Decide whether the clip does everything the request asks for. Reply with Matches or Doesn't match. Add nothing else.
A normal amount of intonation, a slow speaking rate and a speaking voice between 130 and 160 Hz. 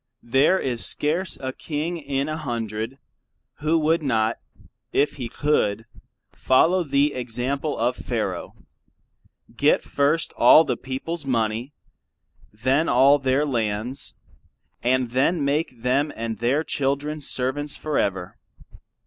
Matches